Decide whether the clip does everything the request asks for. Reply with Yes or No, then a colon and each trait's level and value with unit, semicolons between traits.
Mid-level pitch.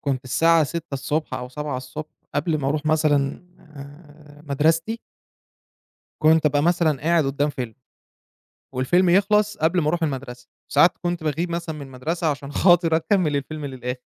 Yes: medium, 150 Hz